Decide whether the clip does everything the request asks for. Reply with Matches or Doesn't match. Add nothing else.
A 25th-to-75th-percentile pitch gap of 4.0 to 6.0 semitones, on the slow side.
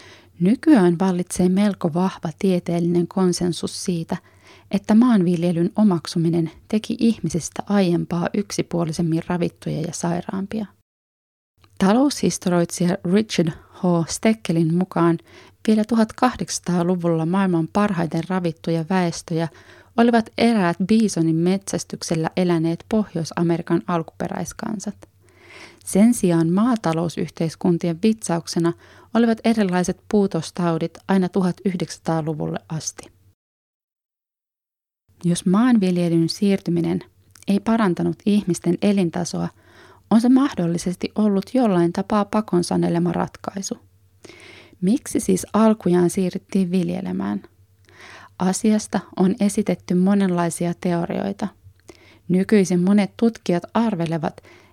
Doesn't match